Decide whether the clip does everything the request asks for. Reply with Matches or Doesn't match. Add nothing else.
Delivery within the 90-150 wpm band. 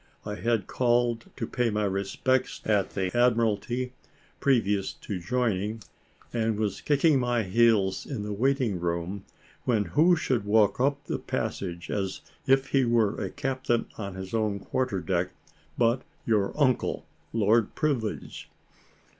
Matches